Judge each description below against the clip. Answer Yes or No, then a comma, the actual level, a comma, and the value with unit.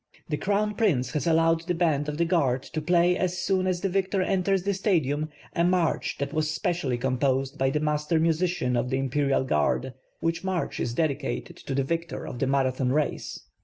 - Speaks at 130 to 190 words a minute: No, average, 200 wpm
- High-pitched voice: No, medium, 155 Hz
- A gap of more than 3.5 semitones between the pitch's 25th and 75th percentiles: Yes, average, 4.7 semitones